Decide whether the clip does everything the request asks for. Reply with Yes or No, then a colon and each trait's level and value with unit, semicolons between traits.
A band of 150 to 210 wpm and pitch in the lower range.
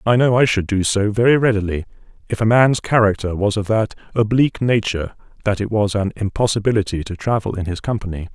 Yes: average, 195 wpm; low, 105 Hz